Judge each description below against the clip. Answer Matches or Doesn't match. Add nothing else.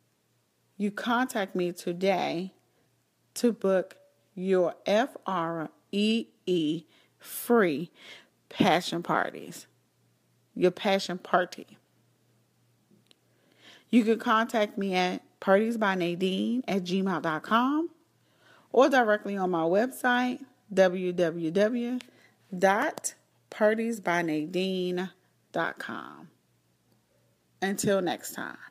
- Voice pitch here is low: Doesn't match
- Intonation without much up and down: Doesn't match